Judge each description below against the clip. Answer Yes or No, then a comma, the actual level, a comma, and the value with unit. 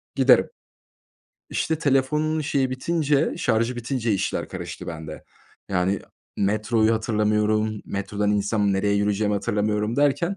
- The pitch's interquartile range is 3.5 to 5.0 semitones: Yes, average, 4.4 semitones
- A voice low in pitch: Yes, low, 110 Hz